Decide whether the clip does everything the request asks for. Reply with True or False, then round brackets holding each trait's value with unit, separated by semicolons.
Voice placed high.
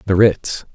False (95 Hz)